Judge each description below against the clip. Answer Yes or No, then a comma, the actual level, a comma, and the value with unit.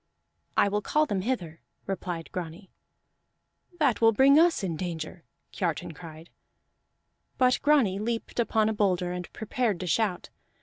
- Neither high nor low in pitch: No, high, 195 Hz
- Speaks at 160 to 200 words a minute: No, average, 140 wpm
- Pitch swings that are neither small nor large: Yes, average, 5.0 semitones